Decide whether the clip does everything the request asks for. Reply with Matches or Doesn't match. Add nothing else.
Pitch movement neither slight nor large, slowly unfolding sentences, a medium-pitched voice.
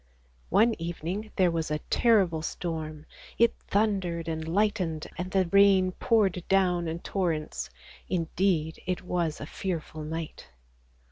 Matches